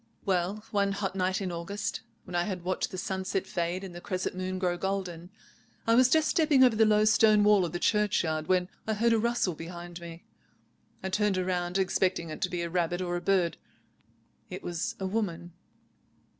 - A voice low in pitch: No, medium, 185 Hz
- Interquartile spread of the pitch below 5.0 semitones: Yes, average, 3.0 semitones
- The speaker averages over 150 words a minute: Yes, average, 200 wpm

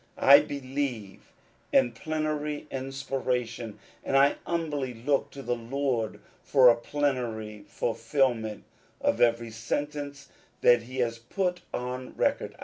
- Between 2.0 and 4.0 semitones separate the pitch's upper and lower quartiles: Yes, average, 3.4 semitones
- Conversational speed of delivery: No, slow, 120 wpm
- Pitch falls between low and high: No, low, 130 Hz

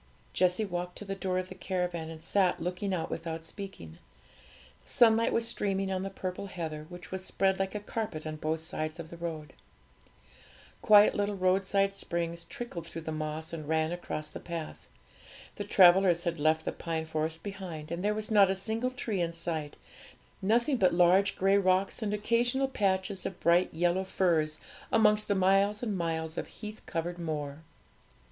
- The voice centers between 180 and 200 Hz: Yes, medium, 185 Hz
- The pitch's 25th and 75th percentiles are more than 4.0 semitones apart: No, average, 3.4 semitones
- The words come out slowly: No, average, 180 wpm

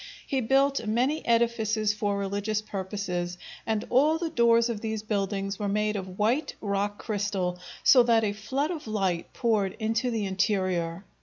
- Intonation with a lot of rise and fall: No, average, 2.9 semitones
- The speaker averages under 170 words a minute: Yes, average, 160 wpm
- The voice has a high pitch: Yes, high, 215 Hz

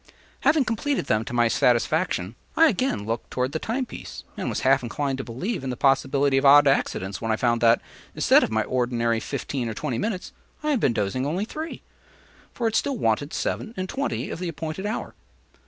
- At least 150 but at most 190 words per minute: No, fast, 205 wpm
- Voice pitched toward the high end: No, low, 135 Hz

